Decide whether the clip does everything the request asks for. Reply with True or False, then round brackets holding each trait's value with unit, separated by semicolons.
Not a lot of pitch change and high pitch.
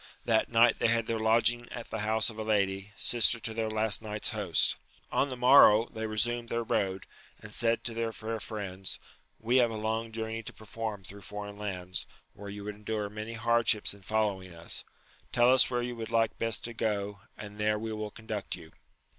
False (1.9 semitones; 110 Hz)